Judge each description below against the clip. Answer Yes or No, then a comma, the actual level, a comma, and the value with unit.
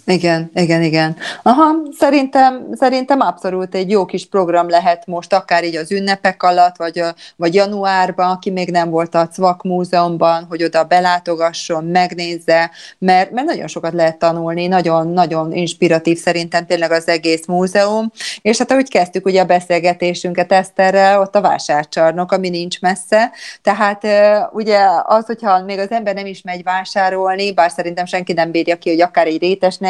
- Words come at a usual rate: No, fast, 165 wpm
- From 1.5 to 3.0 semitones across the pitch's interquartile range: Yes, narrow, 2.5 semitones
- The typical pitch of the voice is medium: Yes, medium, 180 Hz